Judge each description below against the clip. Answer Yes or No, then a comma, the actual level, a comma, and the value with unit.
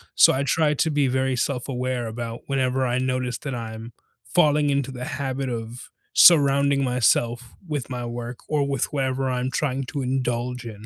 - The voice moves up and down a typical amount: No, narrow, 2.2 semitones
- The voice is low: Yes, low, 130 Hz